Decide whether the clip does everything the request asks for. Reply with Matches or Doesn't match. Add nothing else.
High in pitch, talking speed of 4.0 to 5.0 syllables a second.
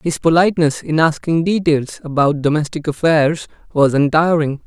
Doesn't match